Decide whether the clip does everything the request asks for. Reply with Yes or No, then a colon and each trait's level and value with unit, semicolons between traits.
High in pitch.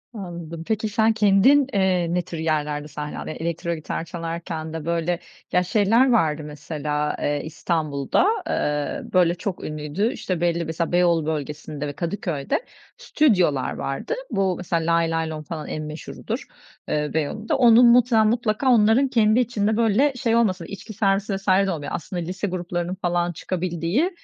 No: medium, 175 Hz